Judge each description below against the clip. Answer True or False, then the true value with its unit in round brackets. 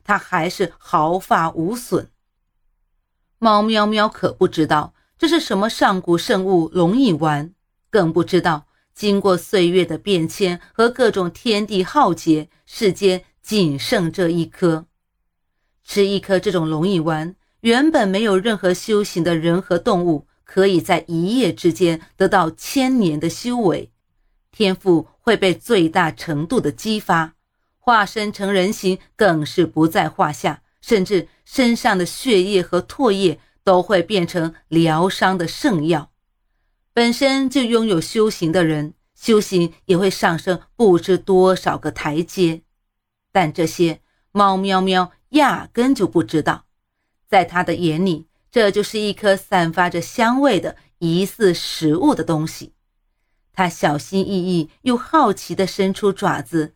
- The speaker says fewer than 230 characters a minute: True (205 characters per minute)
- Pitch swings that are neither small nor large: True (3.7 semitones)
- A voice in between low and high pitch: True (180 Hz)